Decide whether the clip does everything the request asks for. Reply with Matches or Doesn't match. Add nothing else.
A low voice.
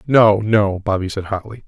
Matches